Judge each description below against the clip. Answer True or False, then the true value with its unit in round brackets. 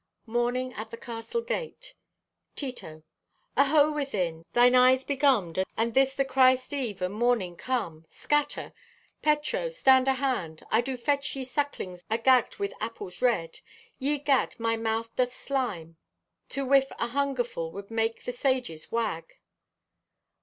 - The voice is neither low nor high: False (250 Hz)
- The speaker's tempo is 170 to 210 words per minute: False (140 wpm)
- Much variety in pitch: False (3.6 semitones)